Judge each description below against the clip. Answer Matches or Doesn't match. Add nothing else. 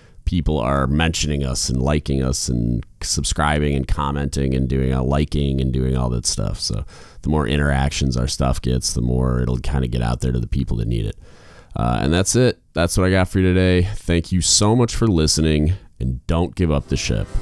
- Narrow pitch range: Doesn't match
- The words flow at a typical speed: Doesn't match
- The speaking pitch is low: Matches